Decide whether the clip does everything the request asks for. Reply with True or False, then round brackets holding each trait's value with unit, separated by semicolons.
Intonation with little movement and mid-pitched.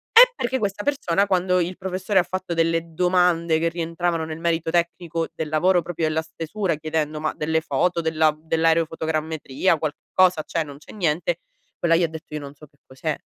True (2.2 semitones; 165 Hz)